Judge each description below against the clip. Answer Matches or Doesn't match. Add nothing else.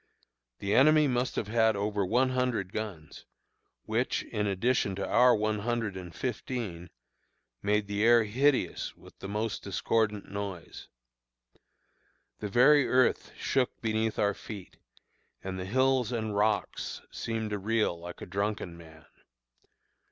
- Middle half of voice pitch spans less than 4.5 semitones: Matches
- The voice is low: Matches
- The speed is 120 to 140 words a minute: Matches